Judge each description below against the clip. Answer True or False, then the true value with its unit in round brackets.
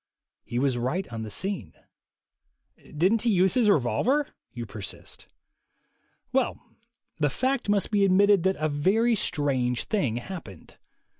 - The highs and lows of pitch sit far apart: True (8.8 semitones)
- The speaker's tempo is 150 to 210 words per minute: False (135 wpm)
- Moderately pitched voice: True (180 Hz)